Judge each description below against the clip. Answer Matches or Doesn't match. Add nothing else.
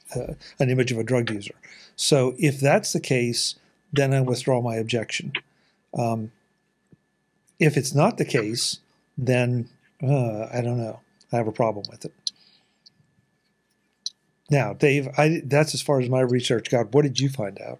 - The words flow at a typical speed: Matches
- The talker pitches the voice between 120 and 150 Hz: Matches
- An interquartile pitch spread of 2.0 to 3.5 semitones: Doesn't match